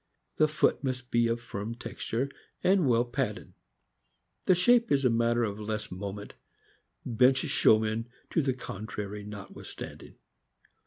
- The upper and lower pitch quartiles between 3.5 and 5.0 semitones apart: Yes, average, 3.8 semitones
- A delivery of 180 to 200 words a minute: No, average, 140 wpm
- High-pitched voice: No, low, 115 Hz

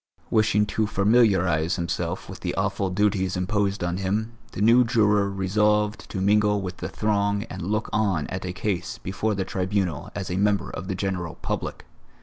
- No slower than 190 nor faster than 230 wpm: No, average, 175 wpm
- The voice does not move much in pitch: Yes, narrow, 2.2 semitones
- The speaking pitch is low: Yes, low, 100 Hz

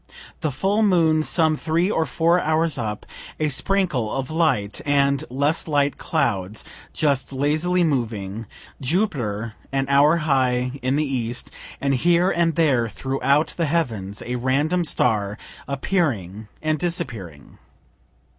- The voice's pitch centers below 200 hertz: Yes, medium, 140 Hz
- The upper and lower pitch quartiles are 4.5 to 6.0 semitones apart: Yes, average, 4.9 semitones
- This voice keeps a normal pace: No, slow, 130 wpm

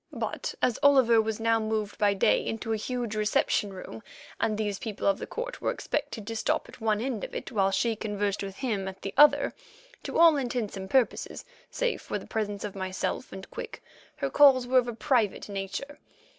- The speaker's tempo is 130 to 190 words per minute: No, fast, 205 wpm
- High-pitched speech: Yes, high, 220 Hz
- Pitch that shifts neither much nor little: Yes, average, 3.8 semitones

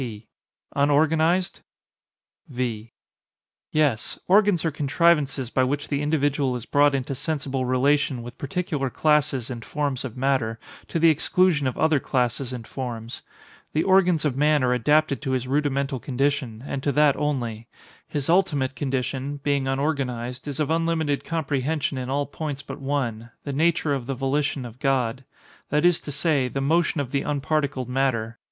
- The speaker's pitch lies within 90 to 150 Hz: Yes, medium, 140 Hz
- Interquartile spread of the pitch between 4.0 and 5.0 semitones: No, average, 2.8 semitones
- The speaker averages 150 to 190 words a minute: Yes, average, 155 wpm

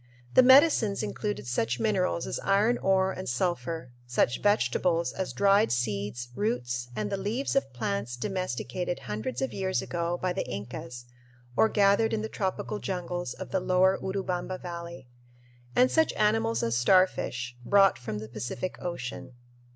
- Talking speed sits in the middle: Yes, average, 150 wpm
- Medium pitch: Yes, medium, 180 Hz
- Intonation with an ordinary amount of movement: No, wide, 8.2 semitones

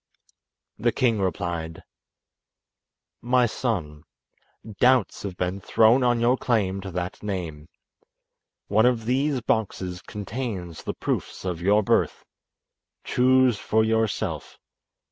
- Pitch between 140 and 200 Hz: No, low, 105 Hz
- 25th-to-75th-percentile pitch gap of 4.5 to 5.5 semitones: Yes, average, 5.0 semitones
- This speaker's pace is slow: Yes, slow, 110 wpm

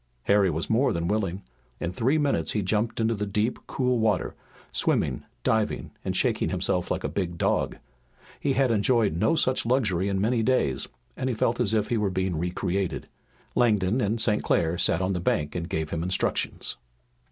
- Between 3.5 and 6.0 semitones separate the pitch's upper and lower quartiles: Yes, average, 4.3 semitones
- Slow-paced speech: No, average, 190 wpm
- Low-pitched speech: Yes, low, 105 Hz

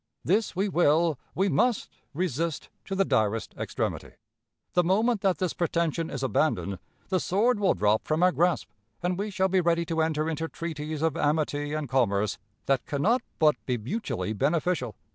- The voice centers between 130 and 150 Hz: No, medium, 165 Hz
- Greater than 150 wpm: Yes, average, 175 wpm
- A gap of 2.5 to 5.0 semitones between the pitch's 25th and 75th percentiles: Yes, average, 4.3 semitones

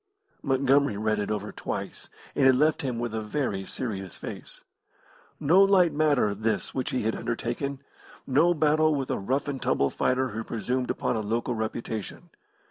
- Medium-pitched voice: No, low, 125 Hz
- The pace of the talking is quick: No, average, 170 wpm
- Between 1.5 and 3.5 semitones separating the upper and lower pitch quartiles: No, average, 4.5 semitones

